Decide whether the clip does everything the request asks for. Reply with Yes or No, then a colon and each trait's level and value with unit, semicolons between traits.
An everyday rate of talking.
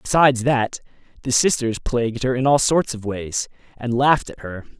Yes: average, 190 wpm